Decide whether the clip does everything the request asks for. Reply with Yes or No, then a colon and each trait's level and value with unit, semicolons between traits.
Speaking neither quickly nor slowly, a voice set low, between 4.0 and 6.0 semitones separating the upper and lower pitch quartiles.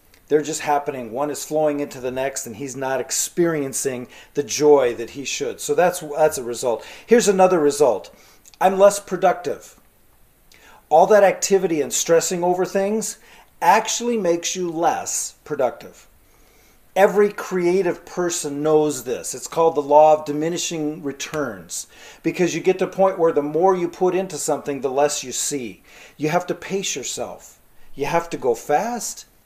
No: average, 165 wpm; medium, 165 Hz; average, 4.4 semitones